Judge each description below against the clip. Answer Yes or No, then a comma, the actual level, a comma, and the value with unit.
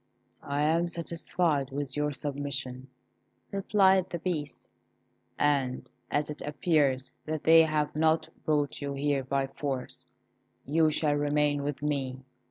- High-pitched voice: No, medium, 145 Hz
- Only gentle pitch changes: Yes, narrow, 2.2 semitones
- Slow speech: Yes, slow, 130 wpm